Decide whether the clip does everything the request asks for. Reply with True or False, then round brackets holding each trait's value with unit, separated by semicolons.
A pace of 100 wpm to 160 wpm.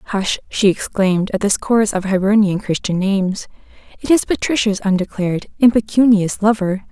True (140 wpm)